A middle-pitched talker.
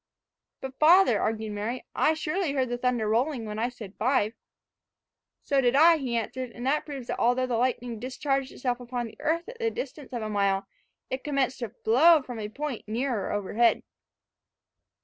No: very high, 250 Hz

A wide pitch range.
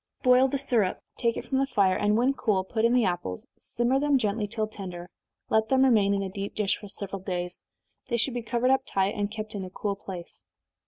No: average, 3.9 semitones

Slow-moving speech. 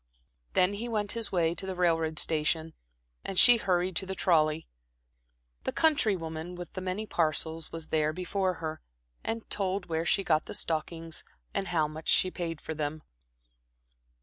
No: average, 170 wpm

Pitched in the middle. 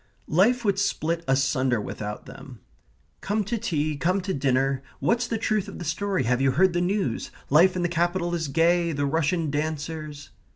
Yes: medium, 165 Hz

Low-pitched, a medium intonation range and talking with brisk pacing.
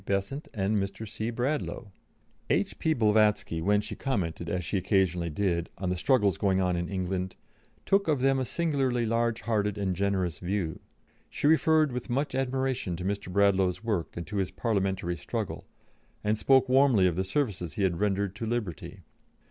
No: low, 100 Hz; average, 4.8 semitones; average, 170 wpm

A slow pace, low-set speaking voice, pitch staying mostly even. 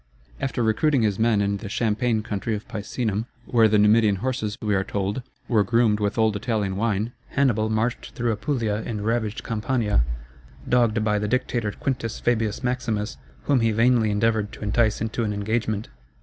No: average, 170 wpm; low, 110 Hz; narrow, 2.2 semitones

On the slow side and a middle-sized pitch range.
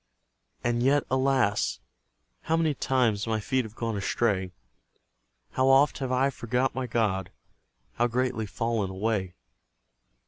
Yes: slow, 130 wpm; average, 3.5 semitones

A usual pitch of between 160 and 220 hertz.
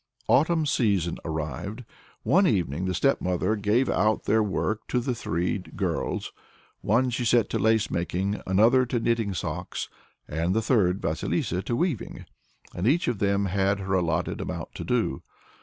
No: low, 100 Hz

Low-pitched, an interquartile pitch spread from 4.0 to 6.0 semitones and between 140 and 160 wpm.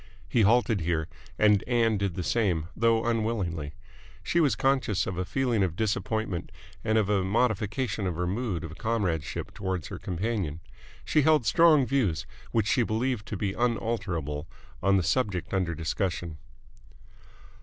Yes: low, 105 Hz; average, 4.6 semitones; average, 155 wpm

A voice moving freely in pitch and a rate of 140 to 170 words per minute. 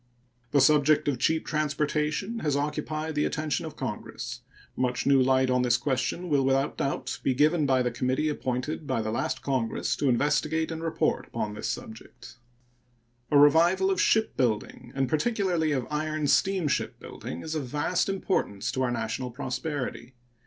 No: average, 3.5 semitones; average, 160 wpm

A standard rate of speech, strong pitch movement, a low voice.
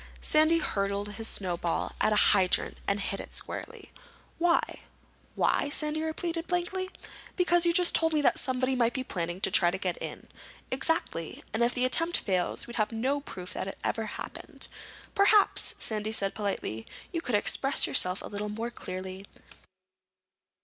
No: average, 165 wpm; wide, 8.2 semitones; high, 230 Hz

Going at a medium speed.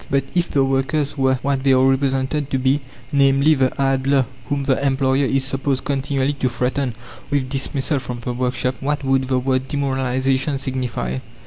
Yes: average, 175 wpm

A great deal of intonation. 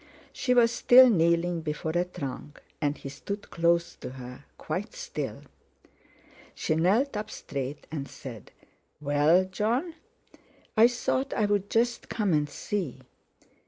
Yes: wide, 7.1 semitones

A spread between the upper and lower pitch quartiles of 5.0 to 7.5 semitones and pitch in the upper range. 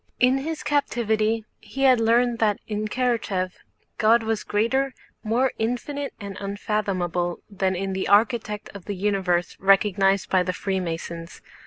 No: average, 3.6 semitones; high, 210 Hz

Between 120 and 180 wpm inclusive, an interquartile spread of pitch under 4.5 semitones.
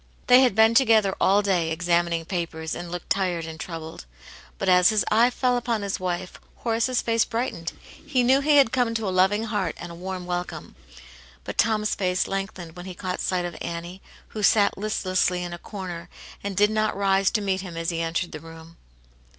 No: average, 200 wpm; average, 3.8 semitones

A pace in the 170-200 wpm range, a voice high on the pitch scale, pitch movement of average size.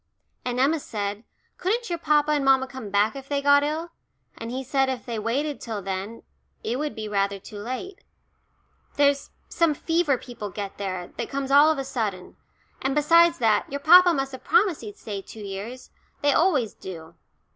No: average, 190 wpm; very high, 265 Hz; wide, 5.9 semitones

